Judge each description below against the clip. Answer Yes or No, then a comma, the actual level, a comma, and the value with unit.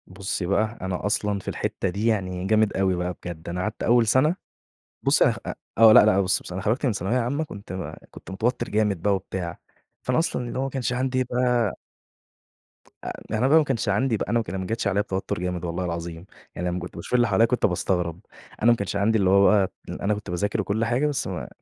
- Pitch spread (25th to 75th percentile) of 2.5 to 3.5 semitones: No, average, 4.3 semitones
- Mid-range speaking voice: No, low, 105 Hz